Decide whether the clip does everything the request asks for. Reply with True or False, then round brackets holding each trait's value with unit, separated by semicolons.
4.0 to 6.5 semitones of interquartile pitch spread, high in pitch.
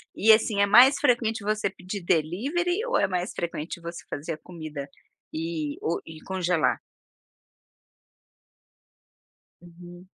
False (4.7 semitones; 180 Hz)